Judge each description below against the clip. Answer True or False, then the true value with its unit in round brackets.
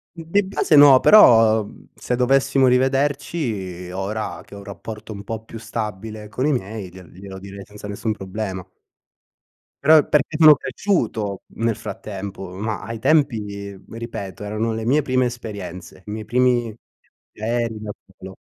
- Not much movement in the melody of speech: False (4.1 semitones)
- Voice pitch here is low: True (110 Hz)